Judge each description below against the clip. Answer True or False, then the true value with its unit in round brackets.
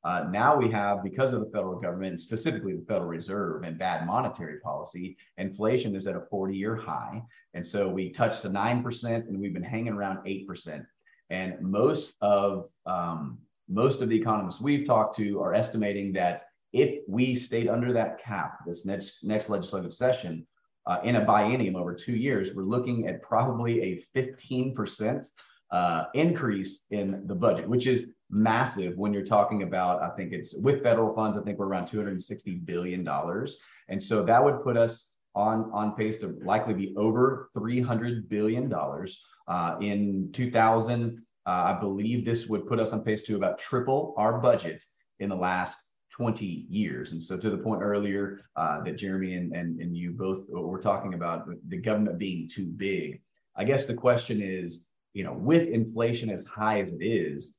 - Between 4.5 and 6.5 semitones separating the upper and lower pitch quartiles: False (3.3 semitones)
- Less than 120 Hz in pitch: True (105 Hz)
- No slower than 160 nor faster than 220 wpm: True (180 wpm)